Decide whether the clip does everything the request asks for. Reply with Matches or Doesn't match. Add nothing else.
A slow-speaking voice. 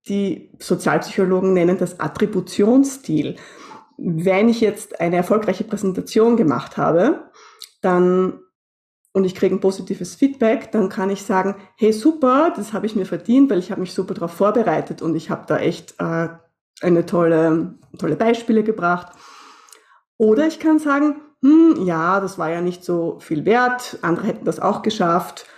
Doesn't match